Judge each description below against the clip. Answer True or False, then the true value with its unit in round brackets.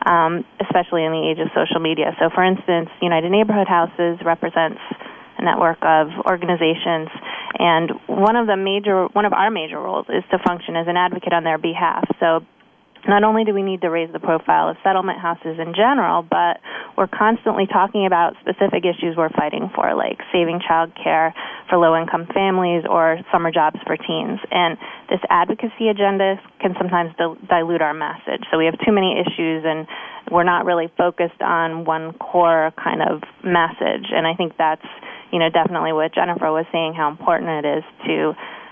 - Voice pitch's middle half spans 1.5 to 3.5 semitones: True (2.4 semitones)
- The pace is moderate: True (180 wpm)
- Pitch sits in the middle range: True (170 Hz)